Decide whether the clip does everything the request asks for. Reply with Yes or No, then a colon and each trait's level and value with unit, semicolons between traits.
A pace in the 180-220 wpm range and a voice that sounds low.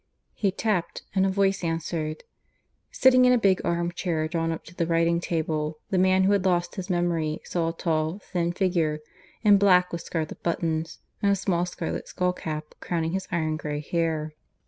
No: average, 190 wpm; medium, 170 Hz